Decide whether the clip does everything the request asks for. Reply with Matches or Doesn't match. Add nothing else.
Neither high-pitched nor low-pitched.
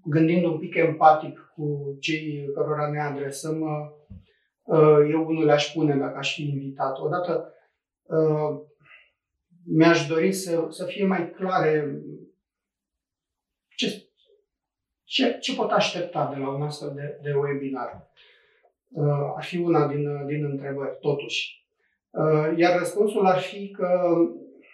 Matches